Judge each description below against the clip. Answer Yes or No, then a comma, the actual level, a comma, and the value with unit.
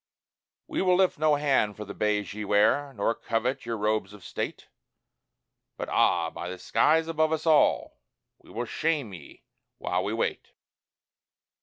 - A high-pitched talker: No, low, 115 Hz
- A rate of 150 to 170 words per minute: Yes, average, 160 wpm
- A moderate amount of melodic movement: No, wide, 6.8 semitones